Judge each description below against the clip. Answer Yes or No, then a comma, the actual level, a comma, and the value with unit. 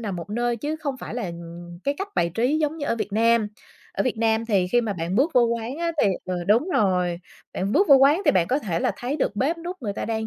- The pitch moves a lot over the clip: Yes, wide, 6.4 semitones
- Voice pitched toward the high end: Yes, high, 230 Hz